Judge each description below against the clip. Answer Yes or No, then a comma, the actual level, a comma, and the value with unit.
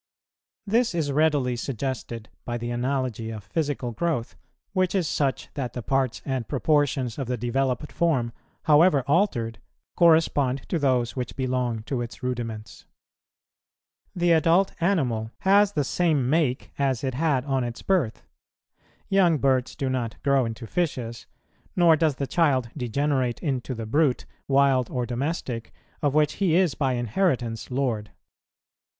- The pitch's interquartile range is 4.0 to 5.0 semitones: Yes, average, 4.5 semitones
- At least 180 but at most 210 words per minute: No, average, 145 wpm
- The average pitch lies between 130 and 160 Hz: Yes, low, 135 Hz